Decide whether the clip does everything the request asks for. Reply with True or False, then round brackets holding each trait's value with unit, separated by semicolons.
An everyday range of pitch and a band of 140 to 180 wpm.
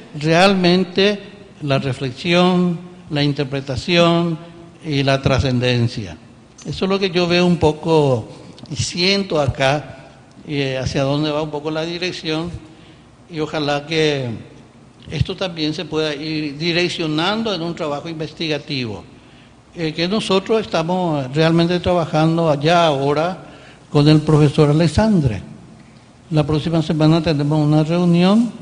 False (3.2 semitones; 120 wpm)